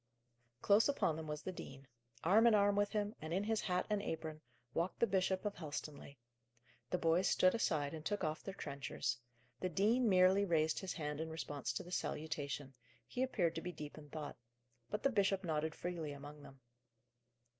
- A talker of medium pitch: Yes, medium, 170 Hz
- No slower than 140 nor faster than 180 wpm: No, average, 190 wpm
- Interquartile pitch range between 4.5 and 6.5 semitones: Yes, average, 4.8 semitones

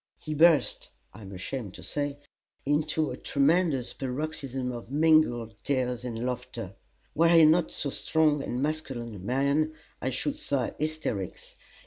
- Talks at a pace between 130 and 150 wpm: Yes, average, 145 wpm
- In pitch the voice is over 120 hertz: Yes, medium, 140 Hz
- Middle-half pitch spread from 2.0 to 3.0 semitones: No, average, 4.1 semitones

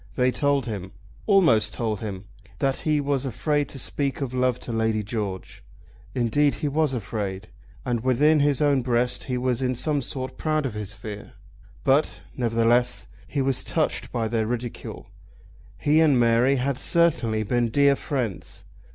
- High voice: No, low, 125 Hz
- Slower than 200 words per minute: Yes, average, 160 wpm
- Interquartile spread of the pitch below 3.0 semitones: No, average, 3.9 semitones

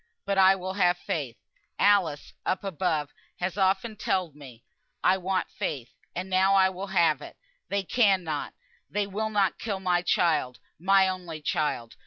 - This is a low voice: No, medium, 185 Hz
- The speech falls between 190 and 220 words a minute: No, average, 160 wpm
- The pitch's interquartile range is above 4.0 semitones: No, average, 3.2 semitones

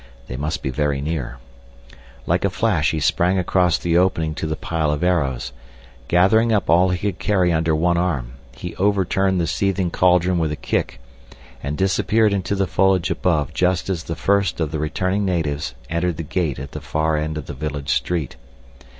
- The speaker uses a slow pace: No, average, 190 wpm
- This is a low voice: Yes, very low, 85 Hz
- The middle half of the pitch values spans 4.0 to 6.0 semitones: No, average, 3.4 semitones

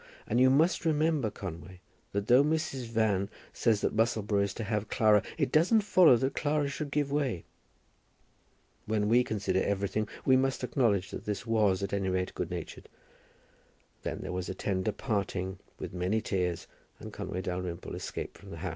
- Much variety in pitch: Yes, wide, 5.7 semitones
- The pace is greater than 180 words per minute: No, average, 175 wpm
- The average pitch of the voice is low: Yes, low, 105 Hz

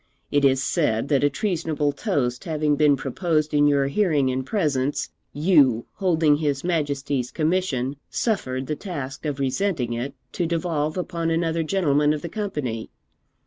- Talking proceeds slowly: No, average, 150 wpm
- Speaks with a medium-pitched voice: Yes, medium, 150 Hz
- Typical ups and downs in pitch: Yes, average, 3.4 semitones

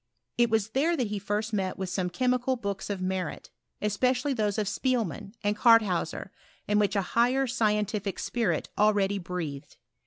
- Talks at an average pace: Yes, average, 165 wpm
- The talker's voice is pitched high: Yes, high, 210 Hz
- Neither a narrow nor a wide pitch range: Yes, average, 3.6 semitones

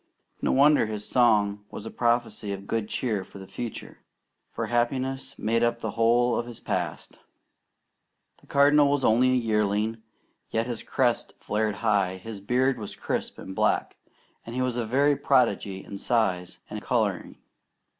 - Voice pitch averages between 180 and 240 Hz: No, low, 115 Hz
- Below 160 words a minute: No, average, 165 wpm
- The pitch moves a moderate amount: Yes, average, 3.2 semitones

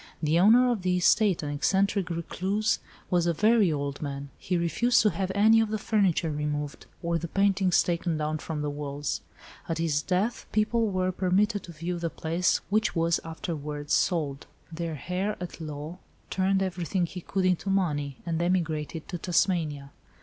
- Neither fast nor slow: Yes, average, 170 wpm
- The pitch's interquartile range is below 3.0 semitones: No, average, 3.8 semitones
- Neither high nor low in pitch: Yes, medium, 175 Hz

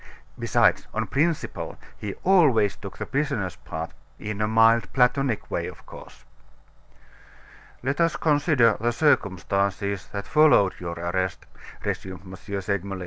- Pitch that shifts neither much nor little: No, wide, 6.4 semitones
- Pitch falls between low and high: No, low, 105 Hz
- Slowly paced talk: Yes, slow, 130 wpm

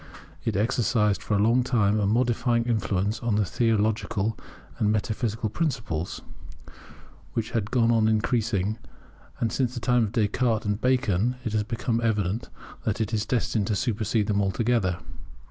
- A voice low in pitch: Yes, low, 110 Hz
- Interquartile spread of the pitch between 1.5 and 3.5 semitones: Yes, narrow, 2.4 semitones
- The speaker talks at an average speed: Yes, average, 150 wpm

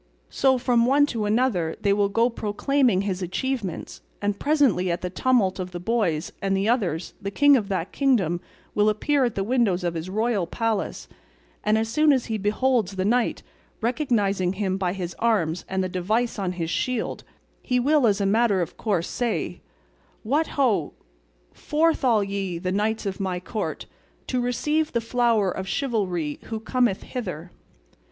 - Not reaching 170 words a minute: No, average, 175 wpm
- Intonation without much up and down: No, average, 4.7 semitones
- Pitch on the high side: Yes, high, 210 Hz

